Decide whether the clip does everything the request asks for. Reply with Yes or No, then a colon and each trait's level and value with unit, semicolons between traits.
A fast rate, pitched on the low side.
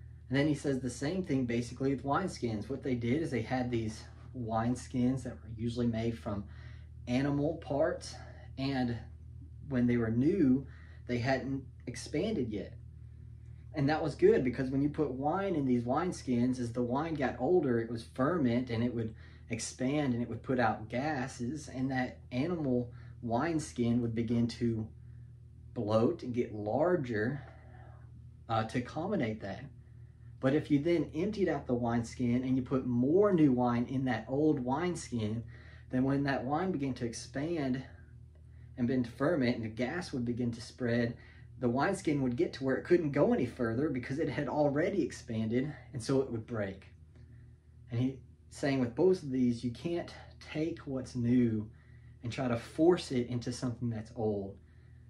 No: average, 170 wpm; low, 120 Hz